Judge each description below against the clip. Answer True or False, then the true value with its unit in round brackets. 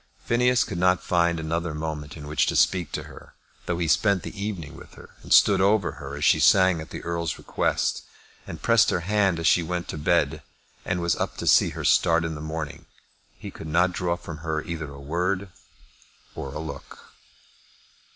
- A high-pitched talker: False (85 Hz)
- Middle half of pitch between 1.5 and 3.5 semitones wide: True (2.8 semitones)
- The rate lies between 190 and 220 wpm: True (200 wpm)